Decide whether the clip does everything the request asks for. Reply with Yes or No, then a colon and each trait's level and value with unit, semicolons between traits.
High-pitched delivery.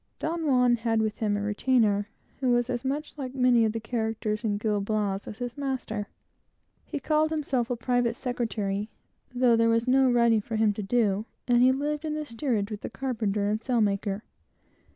Yes: high, 235 Hz